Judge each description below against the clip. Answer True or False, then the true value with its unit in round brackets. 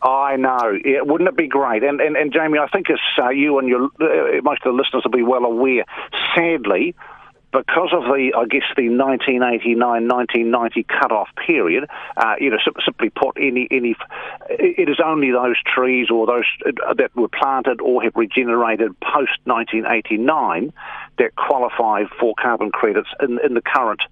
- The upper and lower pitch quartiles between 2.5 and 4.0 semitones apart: False (4.8 semitones)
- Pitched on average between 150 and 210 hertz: False (135 Hz)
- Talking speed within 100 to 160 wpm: False (175 wpm)